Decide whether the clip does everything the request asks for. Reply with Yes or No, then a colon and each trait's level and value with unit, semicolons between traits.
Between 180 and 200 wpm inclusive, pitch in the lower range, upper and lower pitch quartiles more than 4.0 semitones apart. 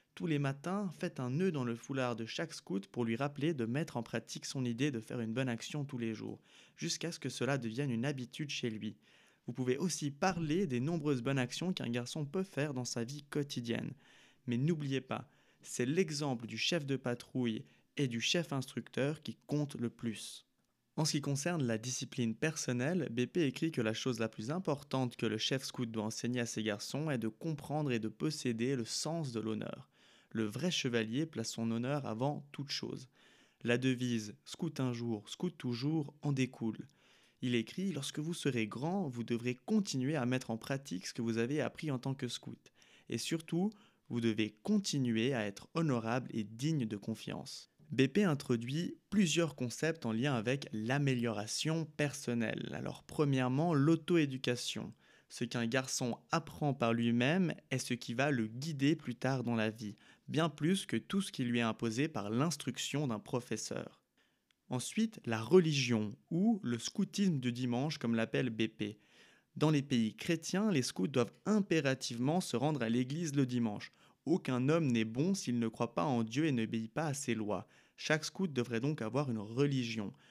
Yes: average, 185 wpm; low, 130 Hz; average, 4.7 semitones